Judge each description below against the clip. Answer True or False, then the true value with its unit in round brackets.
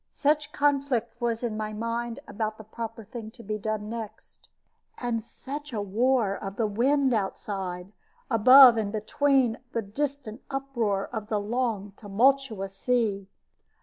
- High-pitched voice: True (230 Hz)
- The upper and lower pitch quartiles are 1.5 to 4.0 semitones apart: True (3.6 semitones)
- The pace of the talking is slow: False (145 wpm)